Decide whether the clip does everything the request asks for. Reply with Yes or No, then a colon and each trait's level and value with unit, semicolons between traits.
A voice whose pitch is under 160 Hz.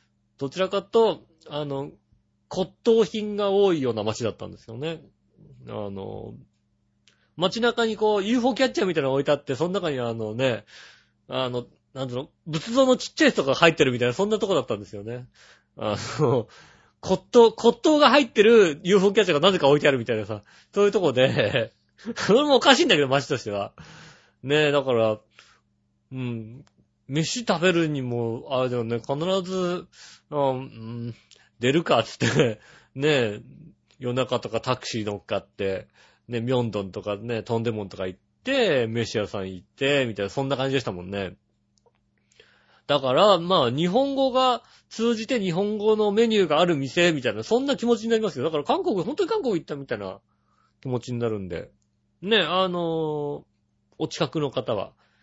Yes: medium, 140 Hz